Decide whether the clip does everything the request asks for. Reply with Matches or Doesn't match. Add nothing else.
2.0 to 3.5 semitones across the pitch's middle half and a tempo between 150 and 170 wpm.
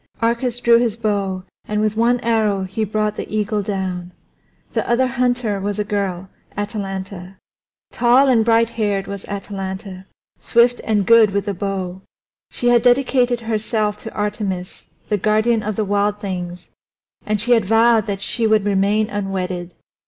Matches